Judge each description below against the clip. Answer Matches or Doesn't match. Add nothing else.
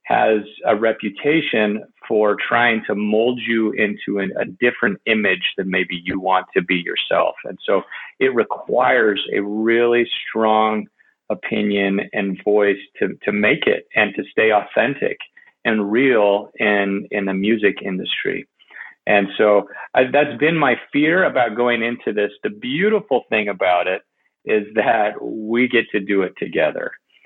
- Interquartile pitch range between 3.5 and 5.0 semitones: Doesn't match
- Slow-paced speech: Doesn't match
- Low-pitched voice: Matches